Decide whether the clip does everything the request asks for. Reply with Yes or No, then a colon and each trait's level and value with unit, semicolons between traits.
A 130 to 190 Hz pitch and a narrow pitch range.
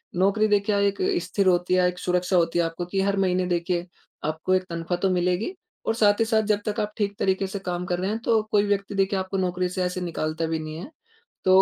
Yes: medium, 185 Hz; narrow, 2.3 semitones